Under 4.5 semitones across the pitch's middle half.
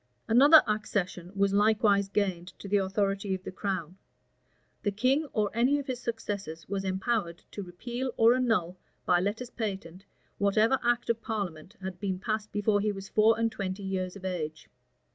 Yes: average, 3.1 semitones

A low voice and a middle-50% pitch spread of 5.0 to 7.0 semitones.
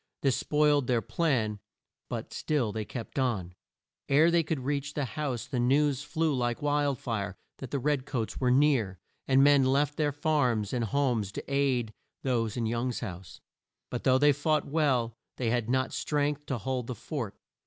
No: low, 130 Hz; average, 3.7 semitones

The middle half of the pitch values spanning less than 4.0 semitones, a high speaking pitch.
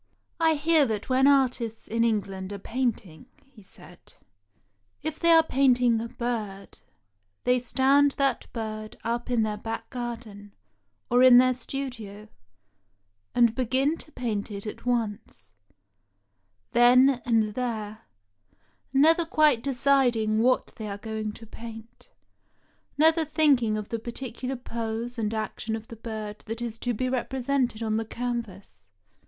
Yes: average, 3.1 semitones; high, 235 Hz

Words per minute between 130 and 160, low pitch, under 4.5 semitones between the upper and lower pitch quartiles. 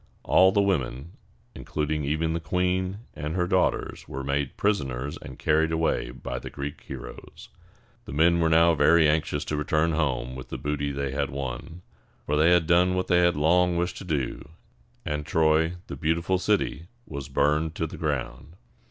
No: average, 180 wpm; very low, 80 Hz; average, 3.4 semitones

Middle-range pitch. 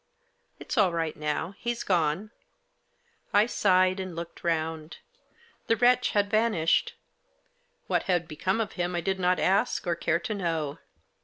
Yes: medium, 180 Hz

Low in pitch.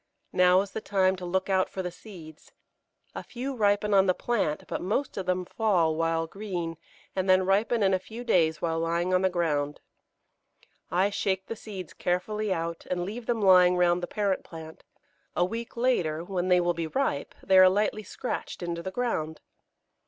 No: medium, 185 Hz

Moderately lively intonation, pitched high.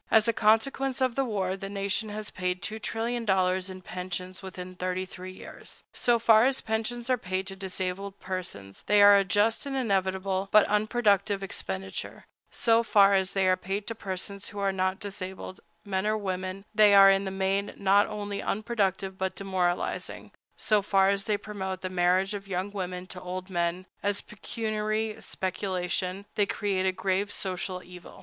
No: narrow, 2.1 semitones; high, 195 Hz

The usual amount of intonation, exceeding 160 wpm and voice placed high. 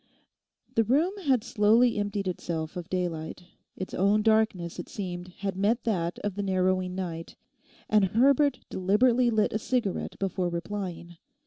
No: average, 3.5 semitones; average, 145 wpm; high, 200 Hz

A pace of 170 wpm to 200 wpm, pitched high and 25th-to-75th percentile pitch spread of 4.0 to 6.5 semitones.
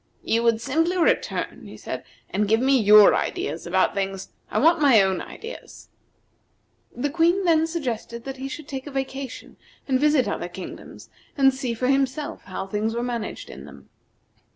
Yes: average, 175 wpm; very high, 260 Hz; average, 5.0 semitones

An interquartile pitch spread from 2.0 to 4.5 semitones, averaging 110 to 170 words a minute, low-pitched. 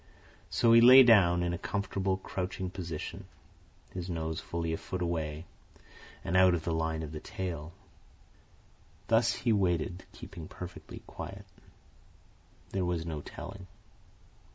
Yes: average, 2.8 semitones; slow, 135 wpm; very low, 90 Hz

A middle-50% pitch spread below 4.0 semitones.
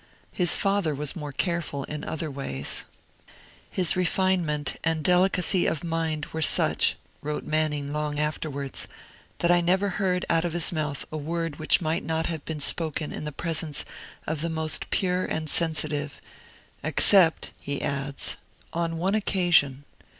Yes: average, 2.7 semitones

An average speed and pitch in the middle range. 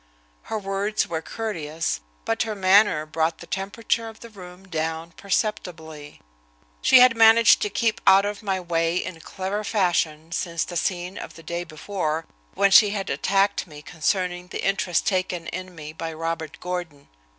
Yes: average, 165 wpm; medium, 180 Hz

